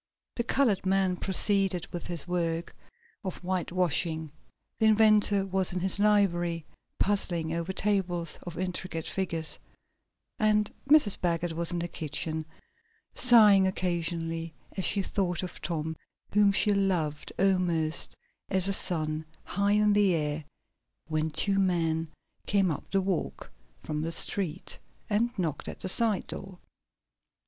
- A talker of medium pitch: Yes, medium, 180 Hz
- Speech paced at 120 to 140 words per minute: Yes, slow, 135 wpm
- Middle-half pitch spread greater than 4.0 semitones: No, average, 3.2 semitones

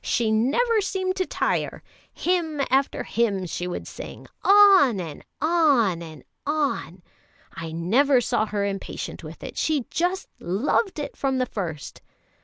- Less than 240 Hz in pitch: No, very high, 260 Hz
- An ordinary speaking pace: Yes, average, 145 wpm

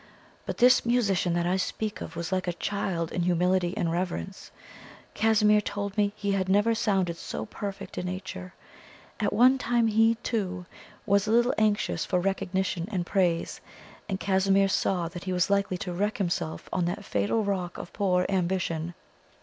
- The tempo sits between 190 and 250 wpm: No, average, 175 wpm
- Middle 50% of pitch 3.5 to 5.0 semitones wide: No, average, 2.7 semitones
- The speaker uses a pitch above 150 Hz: Yes, high, 190 Hz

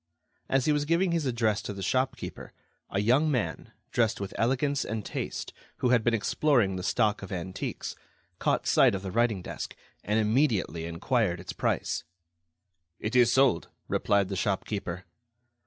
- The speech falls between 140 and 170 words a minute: Yes, average, 160 wpm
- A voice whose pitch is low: Yes, low, 110 Hz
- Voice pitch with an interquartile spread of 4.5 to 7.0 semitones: Yes, average, 4.9 semitones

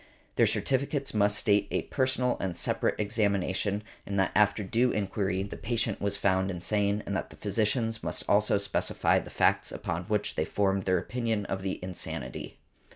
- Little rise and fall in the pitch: Yes, narrow, 2.3 semitones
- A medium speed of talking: Yes, average, 165 wpm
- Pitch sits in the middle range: No, low, 100 Hz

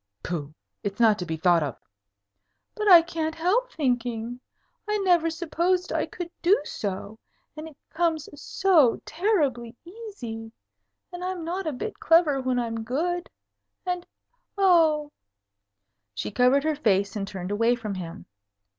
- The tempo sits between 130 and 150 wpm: Yes, average, 145 wpm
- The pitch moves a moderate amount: No, wide, 7.7 semitones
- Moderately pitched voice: No, very high, 295 Hz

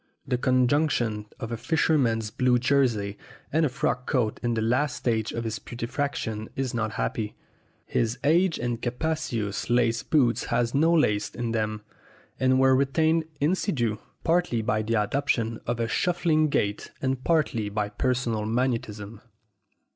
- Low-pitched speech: Yes, low, 120 Hz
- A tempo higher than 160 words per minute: No, average, 150 wpm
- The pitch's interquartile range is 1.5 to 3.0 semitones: No, average, 4.0 semitones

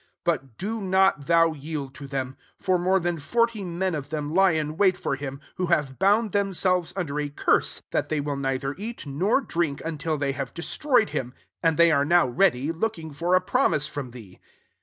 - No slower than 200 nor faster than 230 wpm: Yes, fast, 205 wpm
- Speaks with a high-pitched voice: No, medium, 165 Hz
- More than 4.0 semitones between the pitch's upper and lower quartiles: Yes, average, 4.8 semitones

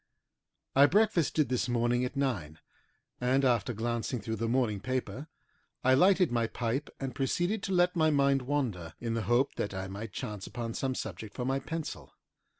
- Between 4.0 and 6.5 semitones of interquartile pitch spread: No, average, 3.6 semitones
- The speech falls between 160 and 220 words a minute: Yes, average, 175 wpm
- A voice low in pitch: Yes, low, 125 Hz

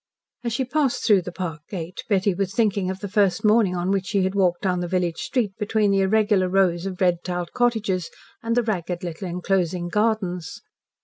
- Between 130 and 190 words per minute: No, average, 200 wpm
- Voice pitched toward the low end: No, high, 190 Hz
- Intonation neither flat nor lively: Yes, average, 3.0 semitones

